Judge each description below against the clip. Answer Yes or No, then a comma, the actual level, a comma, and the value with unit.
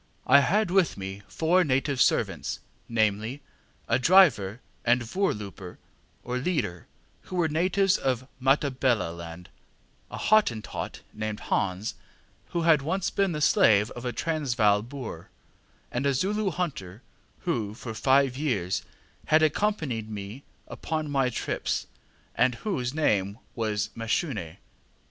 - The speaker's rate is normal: No, slow, 125 wpm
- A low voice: Yes, low, 130 Hz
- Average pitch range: No, wide, 6.8 semitones